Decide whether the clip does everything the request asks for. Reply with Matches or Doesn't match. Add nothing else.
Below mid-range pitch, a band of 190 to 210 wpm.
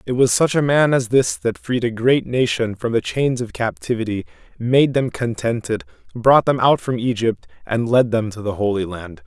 Matches